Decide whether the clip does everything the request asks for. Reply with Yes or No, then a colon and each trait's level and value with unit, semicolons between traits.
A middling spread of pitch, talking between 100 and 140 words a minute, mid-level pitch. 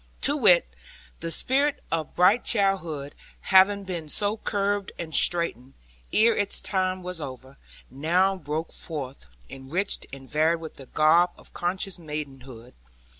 Yes: average, 5.0 semitones; slow, 135 wpm; medium, 170 Hz